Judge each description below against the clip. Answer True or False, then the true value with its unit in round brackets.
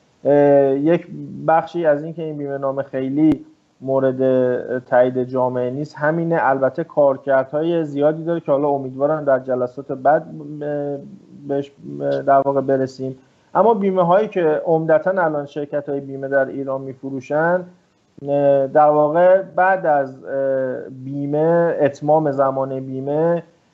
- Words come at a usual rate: True (120 wpm)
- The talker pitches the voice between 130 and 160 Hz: True (140 Hz)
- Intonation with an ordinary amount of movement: True (3.0 semitones)